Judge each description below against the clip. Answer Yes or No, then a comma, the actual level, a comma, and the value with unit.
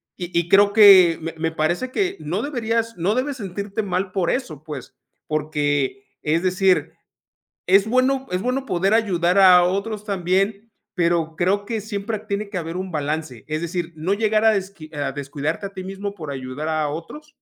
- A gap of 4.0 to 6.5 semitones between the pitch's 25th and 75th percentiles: Yes, average, 4.5 semitones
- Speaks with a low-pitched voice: No, medium, 185 Hz